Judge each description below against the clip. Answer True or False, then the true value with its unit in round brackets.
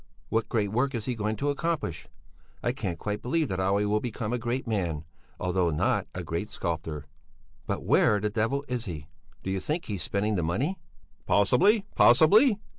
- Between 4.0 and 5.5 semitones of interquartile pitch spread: True (5.2 semitones)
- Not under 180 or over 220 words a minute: True (185 wpm)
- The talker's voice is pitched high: False (105 Hz)